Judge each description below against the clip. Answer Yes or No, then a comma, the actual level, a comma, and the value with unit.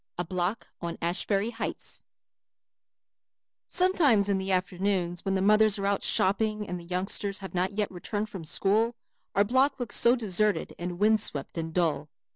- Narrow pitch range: No, average, 3.1 semitones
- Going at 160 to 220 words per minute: Yes, average, 165 wpm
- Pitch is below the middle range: No, high, 195 Hz